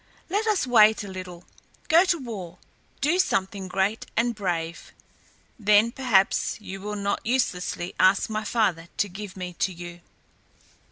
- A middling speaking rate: Yes, average, 150 wpm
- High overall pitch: Yes, high, 205 Hz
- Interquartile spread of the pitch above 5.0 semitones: No, average, 4.0 semitones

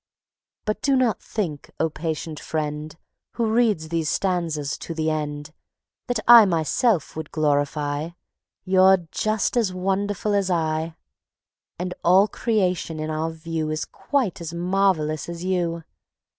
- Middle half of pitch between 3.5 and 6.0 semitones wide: Yes, average, 3.9 semitones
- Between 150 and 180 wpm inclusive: No, slow, 135 wpm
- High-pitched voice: No, medium, 170 Hz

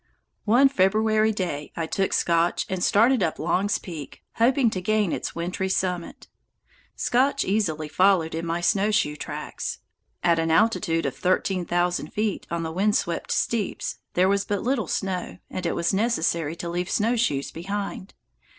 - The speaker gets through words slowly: No, average, 160 wpm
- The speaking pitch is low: No, medium, 185 Hz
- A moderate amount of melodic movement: Yes, average, 4.0 semitones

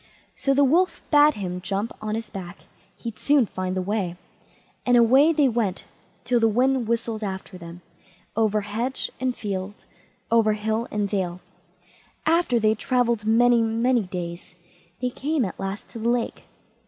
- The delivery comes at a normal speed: Yes, average, 165 wpm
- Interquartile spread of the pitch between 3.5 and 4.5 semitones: Yes, average, 3.9 semitones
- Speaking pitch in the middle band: No, high, 225 Hz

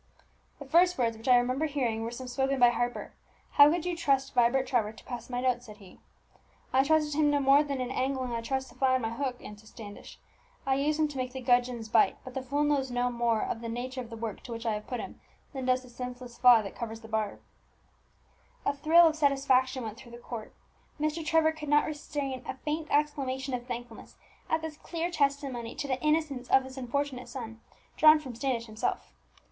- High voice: Yes, very high, 255 Hz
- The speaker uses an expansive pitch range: No, average, 3.1 semitones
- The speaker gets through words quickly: Yes, fast, 220 wpm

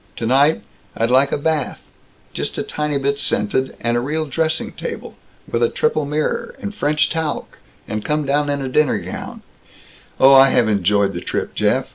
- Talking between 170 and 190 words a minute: Yes, average, 180 wpm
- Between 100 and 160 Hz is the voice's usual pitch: Yes, medium, 140 Hz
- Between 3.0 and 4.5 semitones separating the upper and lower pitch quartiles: Yes, average, 3.6 semitones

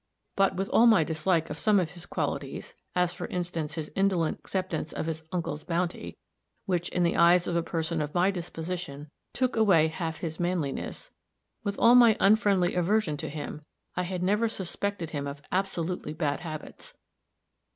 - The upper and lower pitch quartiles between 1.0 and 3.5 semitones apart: Yes, average, 3.1 semitones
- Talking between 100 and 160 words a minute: No, average, 170 wpm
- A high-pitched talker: No, medium, 175 Hz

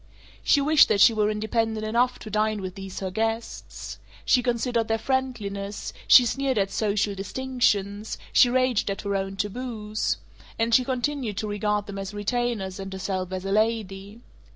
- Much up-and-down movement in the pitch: No, average, 3.4 semitones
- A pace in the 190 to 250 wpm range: No, average, 170 wpm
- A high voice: Yes, high, 215 Hz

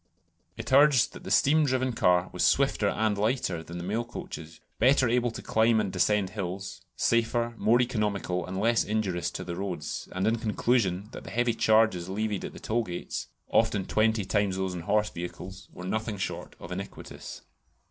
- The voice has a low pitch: Yes, low, 105 Hz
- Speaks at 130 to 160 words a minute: No, average, 185 wpm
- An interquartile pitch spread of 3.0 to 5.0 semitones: Yes, average, 3.9 semitones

